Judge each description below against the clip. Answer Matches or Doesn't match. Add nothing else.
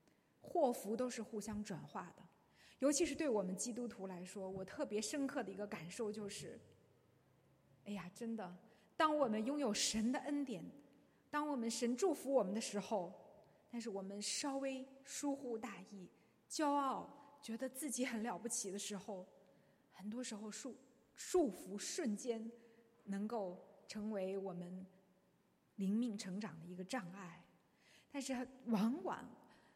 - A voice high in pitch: Matches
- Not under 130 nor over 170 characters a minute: Doesn't match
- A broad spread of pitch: Doesn't match